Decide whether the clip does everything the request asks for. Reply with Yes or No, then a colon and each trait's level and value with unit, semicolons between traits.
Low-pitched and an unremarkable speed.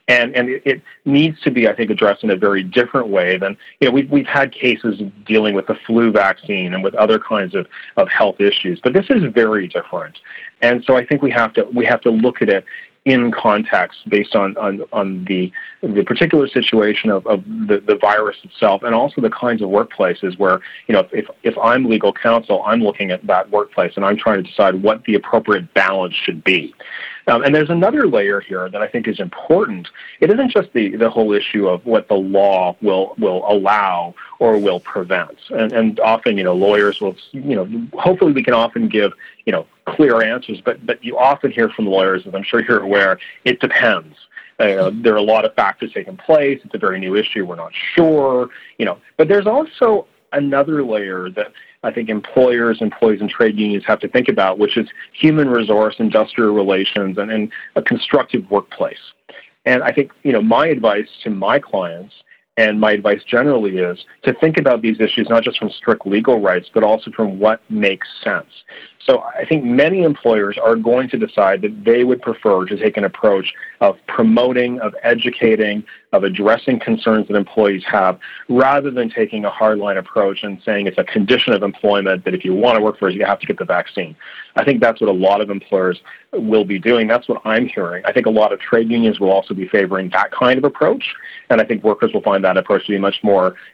No: low, 115 Hz; fast, 215 wpm